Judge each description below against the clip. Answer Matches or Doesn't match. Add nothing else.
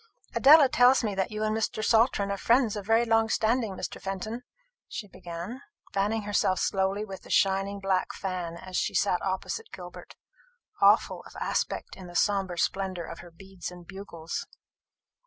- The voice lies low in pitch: Doesn't match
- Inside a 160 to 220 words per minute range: Matches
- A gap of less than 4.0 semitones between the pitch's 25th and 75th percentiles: Matches